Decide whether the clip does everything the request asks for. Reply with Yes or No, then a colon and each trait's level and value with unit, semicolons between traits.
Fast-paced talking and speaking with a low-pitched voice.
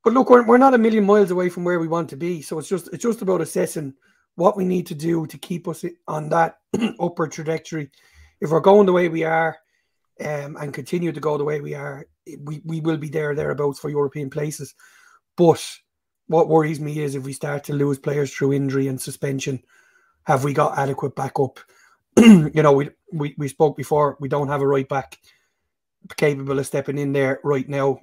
No: fast, 210 wpm; medium, 155 Hz